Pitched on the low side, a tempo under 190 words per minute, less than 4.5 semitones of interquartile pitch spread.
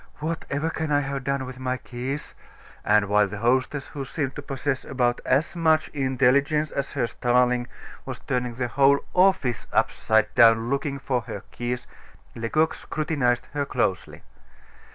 Yes: low, 130 Hz; average, 155 wpm; average, 2.9 semitones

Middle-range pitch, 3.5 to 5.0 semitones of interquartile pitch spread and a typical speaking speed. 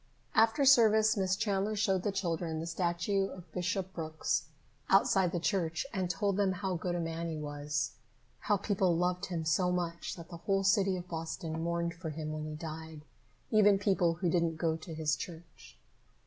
No: medium, 175 Hz; average, 3.1 semitones; average, 190 wpm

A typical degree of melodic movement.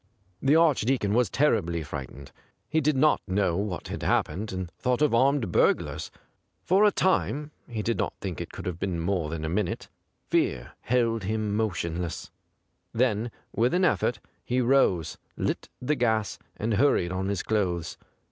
No: wide, 6.2 semitones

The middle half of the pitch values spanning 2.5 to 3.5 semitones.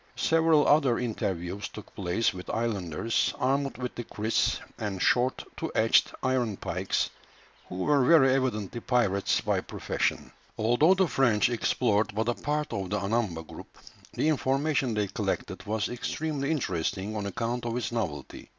No: average, 4.6 semitones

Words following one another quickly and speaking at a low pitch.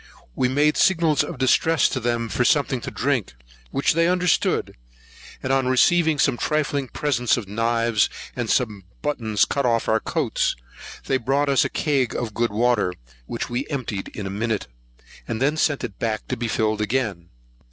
No: average, 175 wpm; low, 125 Hz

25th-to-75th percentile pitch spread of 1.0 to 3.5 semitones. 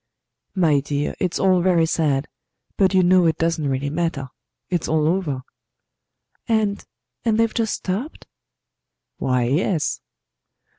No: average, 4.5 semitones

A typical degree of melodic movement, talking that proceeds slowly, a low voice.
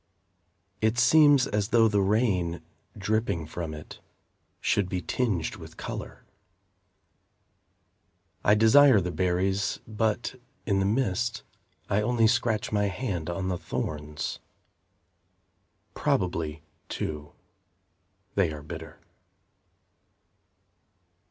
Yes: average, 4.3 semitones; slow, 100 wpm; low, 100 Hz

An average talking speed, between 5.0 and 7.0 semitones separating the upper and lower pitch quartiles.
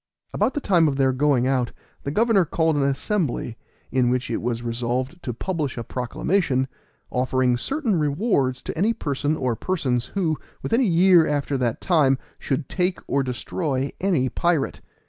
Yes: average, 165 wpm; wide, 5.5 semitones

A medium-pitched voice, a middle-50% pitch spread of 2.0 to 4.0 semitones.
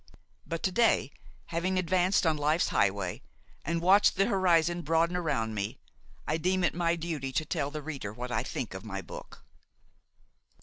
Yes: medium, 165 Hz; average, 3.7 semitones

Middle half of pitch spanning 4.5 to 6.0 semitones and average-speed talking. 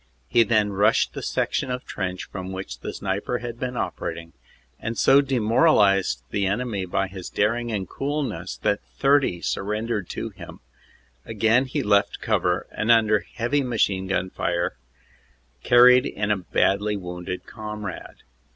No: average, 4.1 semitones; average, 145 wpm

